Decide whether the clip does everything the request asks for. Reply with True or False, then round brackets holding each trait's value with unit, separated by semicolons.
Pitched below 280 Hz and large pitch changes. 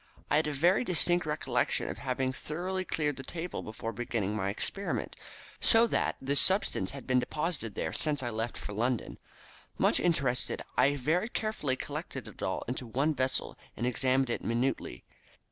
False (135 Hz; 4.8 semitones)